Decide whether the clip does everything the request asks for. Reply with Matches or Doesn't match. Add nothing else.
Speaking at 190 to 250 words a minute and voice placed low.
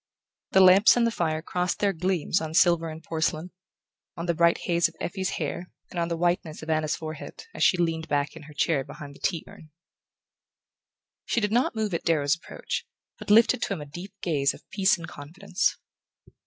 Doesn't match